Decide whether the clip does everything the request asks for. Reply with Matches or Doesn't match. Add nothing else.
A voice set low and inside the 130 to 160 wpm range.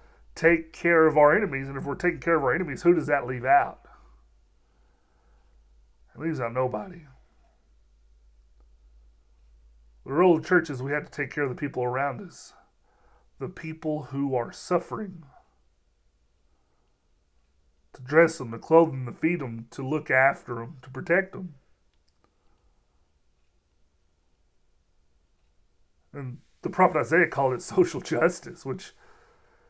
Matches